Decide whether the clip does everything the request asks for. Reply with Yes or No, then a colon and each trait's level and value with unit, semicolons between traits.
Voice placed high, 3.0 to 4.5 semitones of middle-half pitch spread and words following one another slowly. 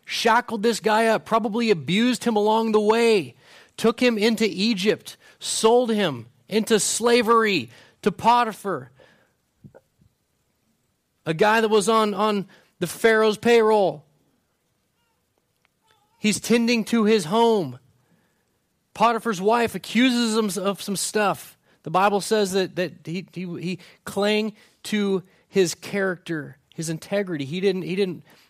Yes: high, 210 Hz; average, 3.8 semitones; slow, 125 wpm